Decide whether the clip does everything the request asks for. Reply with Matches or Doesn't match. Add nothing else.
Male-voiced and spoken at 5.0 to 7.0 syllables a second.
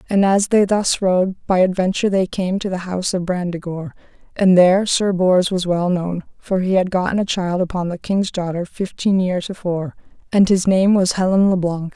Doesn't match